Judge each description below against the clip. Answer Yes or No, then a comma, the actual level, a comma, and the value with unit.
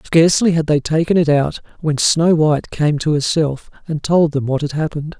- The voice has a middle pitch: Yes, medium, 155 Hz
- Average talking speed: No, fast, 210 wpm